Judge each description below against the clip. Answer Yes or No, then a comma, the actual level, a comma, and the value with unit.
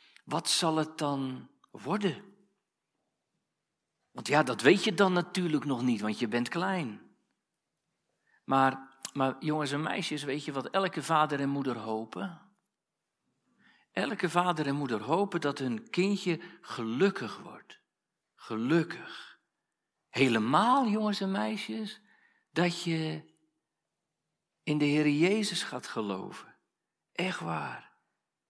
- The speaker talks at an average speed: No, slow, 120 wpm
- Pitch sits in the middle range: Yes, medium, 165 Hz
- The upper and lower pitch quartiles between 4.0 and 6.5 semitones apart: Yes, average, 5.3 semitones